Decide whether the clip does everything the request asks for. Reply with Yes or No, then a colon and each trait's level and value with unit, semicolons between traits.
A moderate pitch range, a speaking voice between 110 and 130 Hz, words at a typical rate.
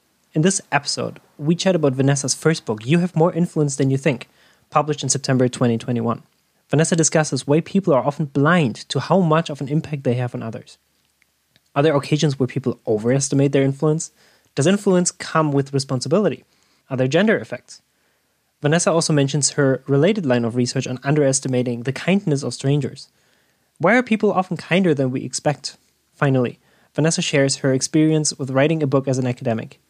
No: average, 3.4 semitones; medium, 140 Hz; average, 175 wpm